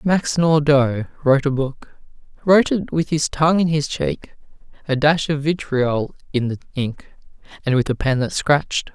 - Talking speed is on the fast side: No, average, 170 wpm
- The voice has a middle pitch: Yes, medium, 145 Hz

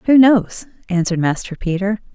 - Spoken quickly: No, average, 140 wpm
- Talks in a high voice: Yes, high, 195 Hz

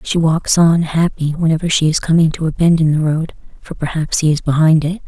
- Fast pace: Yes, fast, 235 wpm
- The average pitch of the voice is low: No, medium, 160 Hz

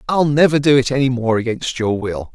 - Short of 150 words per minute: No, fast, 230 wpm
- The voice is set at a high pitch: No, low, 130 Hz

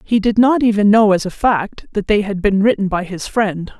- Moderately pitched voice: No, high, 205 Hz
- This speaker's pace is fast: Yes, fast, 255 wpm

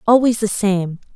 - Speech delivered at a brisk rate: No, average, 155 wpm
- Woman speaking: Yes, female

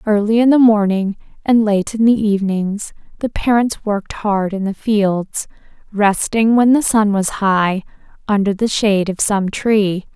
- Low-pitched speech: No, high, 210 Hz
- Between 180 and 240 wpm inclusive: No, average, 165 wpm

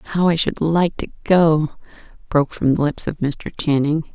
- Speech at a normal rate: Yes, average, 190 wpm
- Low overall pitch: No, medium, 155 Hz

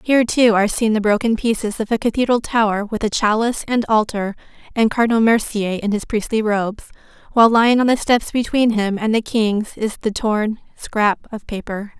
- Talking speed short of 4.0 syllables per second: No, 5.4 syllables/s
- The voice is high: Yes, high, 220 Hz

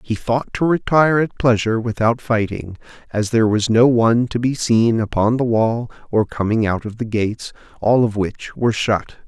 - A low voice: Yes, low, 115 Hz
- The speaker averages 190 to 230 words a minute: Yes, average, 195 wpm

